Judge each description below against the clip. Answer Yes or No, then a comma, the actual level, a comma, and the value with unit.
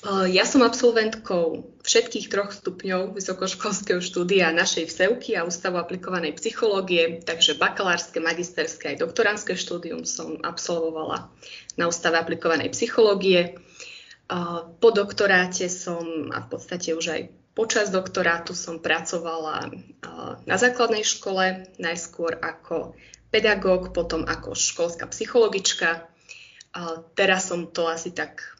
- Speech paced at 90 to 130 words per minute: Yes, slow, 110 wpm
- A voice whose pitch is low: No, medium, 180 Hz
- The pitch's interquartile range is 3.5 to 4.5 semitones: No, average, 3.1 semitones